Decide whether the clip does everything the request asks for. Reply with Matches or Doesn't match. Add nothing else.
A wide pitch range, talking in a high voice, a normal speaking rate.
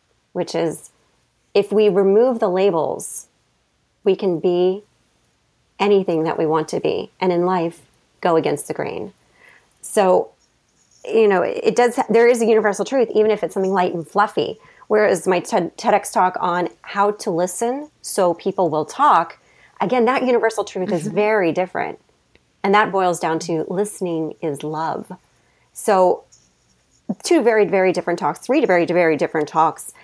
Doesn't match